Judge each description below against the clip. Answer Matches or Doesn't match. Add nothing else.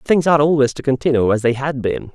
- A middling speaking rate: Doesn't match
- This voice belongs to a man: Matches